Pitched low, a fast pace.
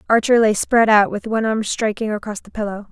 No: high, 215 Hz; fast, 225 wpm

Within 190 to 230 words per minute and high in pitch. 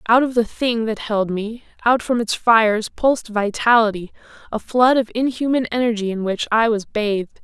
No: average, 180 wpm; high, 225 Hz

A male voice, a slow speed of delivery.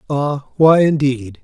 Yes: male; slow, 125 wpm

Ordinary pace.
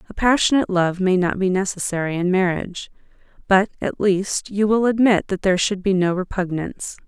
Yes: average, 180 wpm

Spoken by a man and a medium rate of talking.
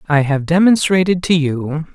Yes: male; average, 155 wpm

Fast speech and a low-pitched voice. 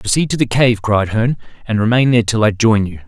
Yes: fast, 255 wpm; low, 110 Hz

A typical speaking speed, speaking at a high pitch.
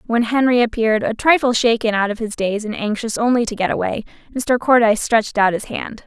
No: fast, 220 wpm; high, 225 Hz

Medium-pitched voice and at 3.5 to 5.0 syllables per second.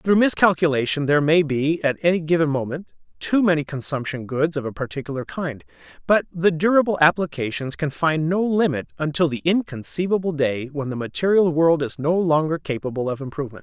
No: medium, 155 Hz; 5.6 syllables/s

